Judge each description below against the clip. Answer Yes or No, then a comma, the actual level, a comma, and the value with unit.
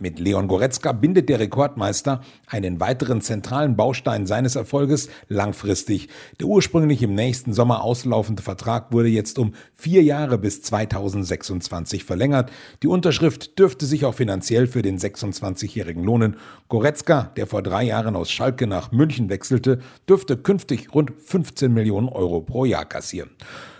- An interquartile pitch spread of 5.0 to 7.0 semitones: Yes, average, 5.3 semitones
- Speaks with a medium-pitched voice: No, low, 120 Hz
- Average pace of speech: Yes, average, 145 wpm